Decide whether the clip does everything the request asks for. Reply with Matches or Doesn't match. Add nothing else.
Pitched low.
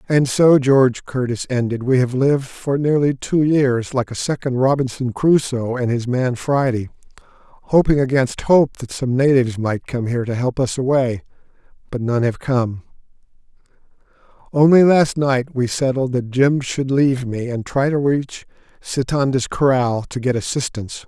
Matches